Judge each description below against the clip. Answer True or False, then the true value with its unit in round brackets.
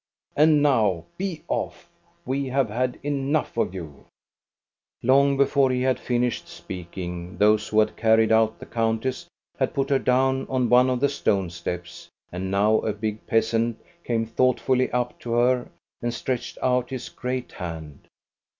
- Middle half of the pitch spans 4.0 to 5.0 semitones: False (3.5 semitones)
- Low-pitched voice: True (120 Hz)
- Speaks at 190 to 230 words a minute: False (160 wpm)